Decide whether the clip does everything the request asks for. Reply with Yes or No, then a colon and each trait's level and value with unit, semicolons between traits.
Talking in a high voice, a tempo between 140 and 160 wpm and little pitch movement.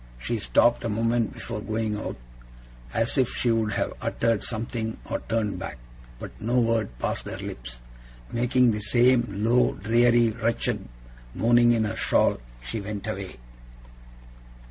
No: low, 115 Hz; average, 145 wpm; narrow, 2.0 semitones